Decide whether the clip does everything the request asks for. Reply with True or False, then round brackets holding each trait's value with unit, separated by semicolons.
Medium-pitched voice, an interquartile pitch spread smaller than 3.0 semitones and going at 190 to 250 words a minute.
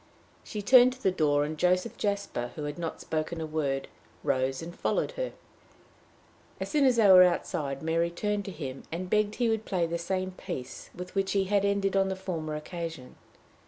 False (180 Hz; 4.3 semitones; 200 wpm)